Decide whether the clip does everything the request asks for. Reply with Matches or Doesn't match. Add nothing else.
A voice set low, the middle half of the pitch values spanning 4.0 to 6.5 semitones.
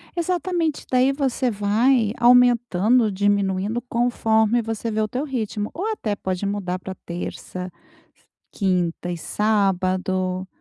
Doesn't match